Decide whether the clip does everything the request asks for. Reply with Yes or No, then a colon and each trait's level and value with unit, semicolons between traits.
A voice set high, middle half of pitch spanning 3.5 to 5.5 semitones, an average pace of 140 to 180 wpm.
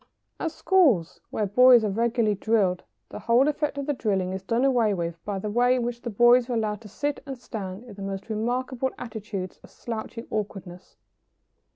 No: high, 225 Hz; average, 3.9 semitones; average, 200 wpm